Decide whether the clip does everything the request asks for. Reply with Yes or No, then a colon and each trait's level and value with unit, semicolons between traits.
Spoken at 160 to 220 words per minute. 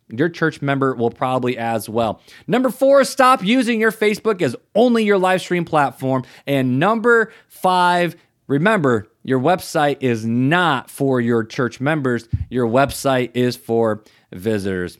No: average, 145 wpm